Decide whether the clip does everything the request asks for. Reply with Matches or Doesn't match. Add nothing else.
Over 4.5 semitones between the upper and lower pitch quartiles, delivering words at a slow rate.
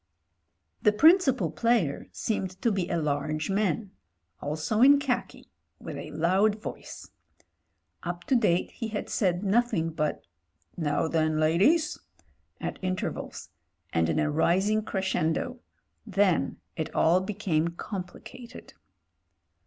Matches